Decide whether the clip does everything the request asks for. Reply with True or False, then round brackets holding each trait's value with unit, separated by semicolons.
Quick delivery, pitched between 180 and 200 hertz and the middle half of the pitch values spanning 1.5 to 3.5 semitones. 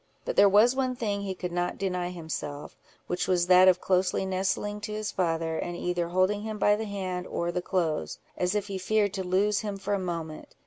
True (220 wpm; 185 Hz; 2.6 semitones)